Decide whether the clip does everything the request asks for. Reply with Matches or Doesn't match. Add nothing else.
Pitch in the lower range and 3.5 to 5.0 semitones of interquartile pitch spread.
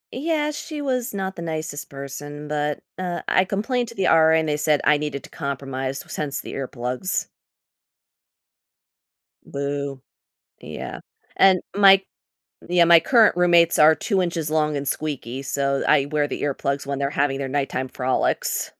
Doesn't match